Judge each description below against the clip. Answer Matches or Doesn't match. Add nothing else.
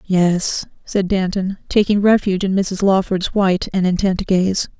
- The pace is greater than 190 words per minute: Doesn't match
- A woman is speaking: Matches